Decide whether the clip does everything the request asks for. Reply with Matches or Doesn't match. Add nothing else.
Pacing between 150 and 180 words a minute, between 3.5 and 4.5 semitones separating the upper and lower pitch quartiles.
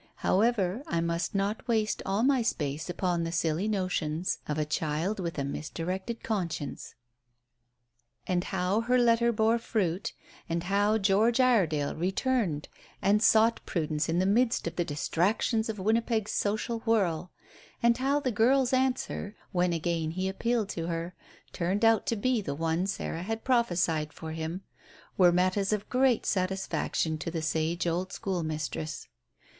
Doesn't match